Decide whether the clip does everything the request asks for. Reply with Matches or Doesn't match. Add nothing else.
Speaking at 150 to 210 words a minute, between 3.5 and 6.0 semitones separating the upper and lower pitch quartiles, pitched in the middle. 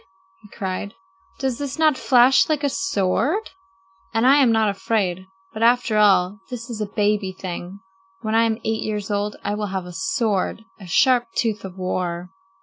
Doesn't match